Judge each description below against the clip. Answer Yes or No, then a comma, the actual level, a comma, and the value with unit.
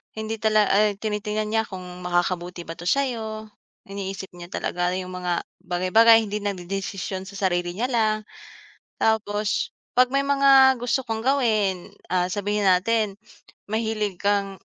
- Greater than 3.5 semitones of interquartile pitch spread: No, average, 3.2 semitones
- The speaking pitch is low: No, high, 205 Hz